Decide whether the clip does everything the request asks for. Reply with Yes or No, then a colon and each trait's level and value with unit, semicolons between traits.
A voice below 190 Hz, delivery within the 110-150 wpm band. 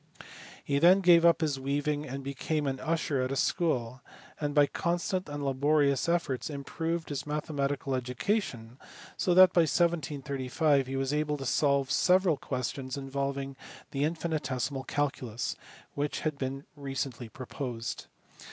Yes: medium, 140 Hz; average, 145 wpm